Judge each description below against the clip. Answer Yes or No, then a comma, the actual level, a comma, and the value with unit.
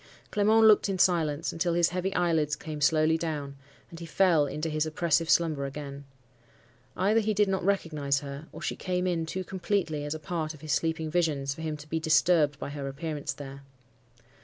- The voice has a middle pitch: Yes, medium, 160 Hz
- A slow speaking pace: No, average, 195 wpm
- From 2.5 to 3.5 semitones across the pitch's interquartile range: Yes, average, 3.1 semitones